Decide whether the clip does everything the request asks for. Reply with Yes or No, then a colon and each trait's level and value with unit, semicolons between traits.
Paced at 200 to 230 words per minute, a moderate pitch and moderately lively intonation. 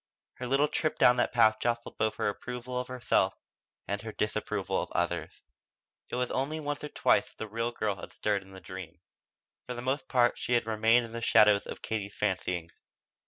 No: fast, 205 wpm; low, 115 Hz; average, 3.2 semitones